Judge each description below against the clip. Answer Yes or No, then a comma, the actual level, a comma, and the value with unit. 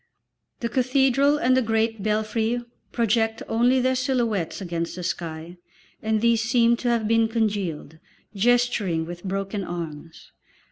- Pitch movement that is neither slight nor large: Yes, average, 4.4 semitones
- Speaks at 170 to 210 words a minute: No, slow, 135 wpm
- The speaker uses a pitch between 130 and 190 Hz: No, high, 225 Hz